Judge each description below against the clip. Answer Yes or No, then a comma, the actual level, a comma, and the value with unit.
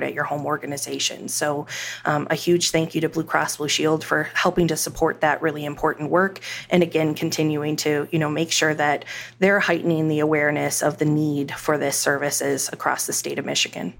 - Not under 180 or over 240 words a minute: Yes, average, 200 wpm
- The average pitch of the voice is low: No, medium, 155 Hz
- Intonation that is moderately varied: No, narrow, 1.8 semitones